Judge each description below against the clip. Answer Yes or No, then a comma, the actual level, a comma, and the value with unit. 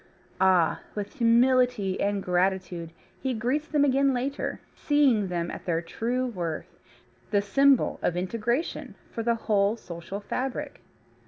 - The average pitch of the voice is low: No, high, 220 Hz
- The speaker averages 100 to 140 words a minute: Yes, slow, 135 wpm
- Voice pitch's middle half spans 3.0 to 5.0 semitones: No, wide, 5.5 semitones